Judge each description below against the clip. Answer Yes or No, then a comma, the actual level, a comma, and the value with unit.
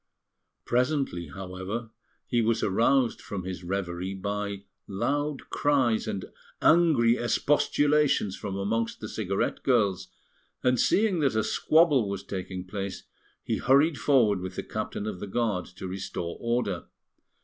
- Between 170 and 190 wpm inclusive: No, slow, 135 wpm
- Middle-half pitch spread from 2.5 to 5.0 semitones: No, wide, 5.5 semitones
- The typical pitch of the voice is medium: No, low, 110 Hz